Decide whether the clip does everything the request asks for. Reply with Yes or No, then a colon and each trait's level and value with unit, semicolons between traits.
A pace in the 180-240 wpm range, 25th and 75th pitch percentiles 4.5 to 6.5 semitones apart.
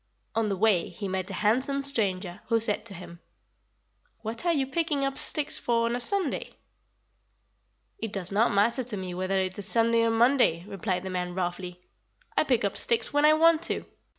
Yes: average, 190 wpm; wide, 5.5 semitones